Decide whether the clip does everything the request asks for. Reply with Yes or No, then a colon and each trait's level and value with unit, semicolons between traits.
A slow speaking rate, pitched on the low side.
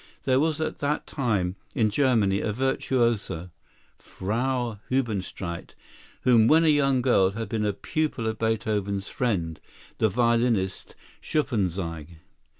Yes: slow, 125 wpm; low, 110 Hz